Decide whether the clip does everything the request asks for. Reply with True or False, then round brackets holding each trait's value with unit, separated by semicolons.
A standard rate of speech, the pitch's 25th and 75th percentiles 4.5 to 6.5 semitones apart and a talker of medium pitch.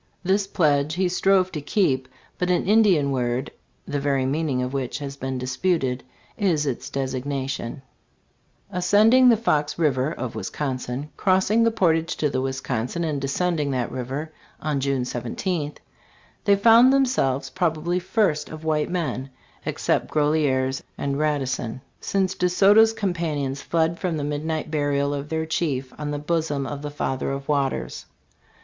True (160 wpm; 4.8 semitones; 150 Hz)